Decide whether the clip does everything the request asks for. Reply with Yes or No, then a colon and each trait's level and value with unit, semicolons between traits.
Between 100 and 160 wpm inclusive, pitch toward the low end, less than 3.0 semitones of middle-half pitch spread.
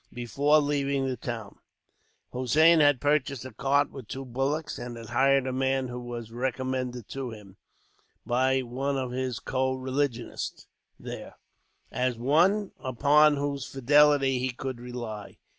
Yes: average, 140 wpm; low, 130 Hz; narrow, 2.4 semitones